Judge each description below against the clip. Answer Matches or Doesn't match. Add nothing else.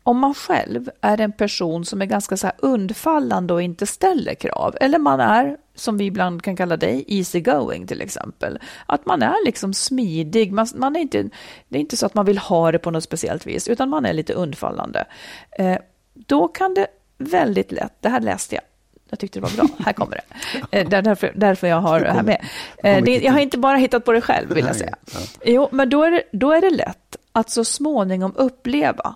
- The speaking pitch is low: Doesn't match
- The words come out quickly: Matches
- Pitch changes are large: Matches